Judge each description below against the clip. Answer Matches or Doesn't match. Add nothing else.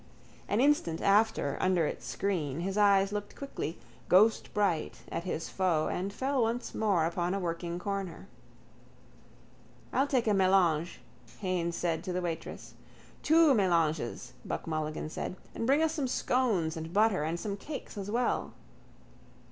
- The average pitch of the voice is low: Doesn't match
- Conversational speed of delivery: Matches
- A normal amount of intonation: Matches